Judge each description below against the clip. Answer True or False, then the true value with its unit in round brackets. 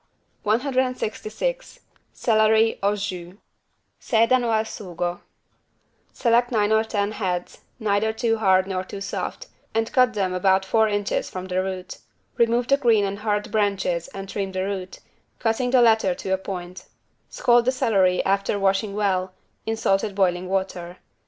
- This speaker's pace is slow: False (150 wpm)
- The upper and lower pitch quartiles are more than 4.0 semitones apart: False (3.0 semitones)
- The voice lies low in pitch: False (205 Hz)